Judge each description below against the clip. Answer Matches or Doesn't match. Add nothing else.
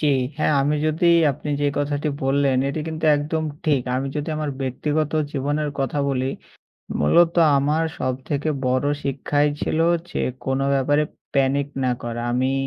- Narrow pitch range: Matches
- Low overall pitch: Doesn't match